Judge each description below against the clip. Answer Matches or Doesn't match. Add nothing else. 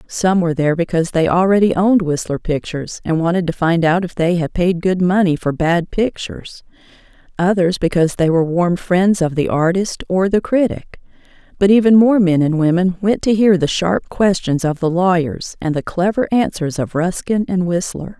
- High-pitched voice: Doesn't match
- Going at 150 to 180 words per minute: Doesn't match